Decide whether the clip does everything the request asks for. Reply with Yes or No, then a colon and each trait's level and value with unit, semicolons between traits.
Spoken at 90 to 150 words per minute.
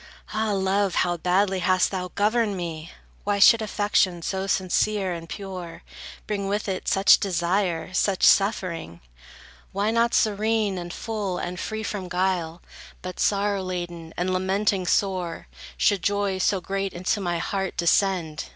Yes: average, 145 wpm